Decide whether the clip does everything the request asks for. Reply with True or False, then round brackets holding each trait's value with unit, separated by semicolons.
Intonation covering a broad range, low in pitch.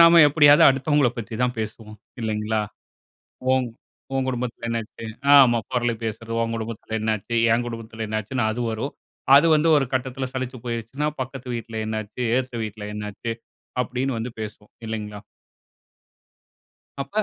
False (3.0 semitones; 115 Hz)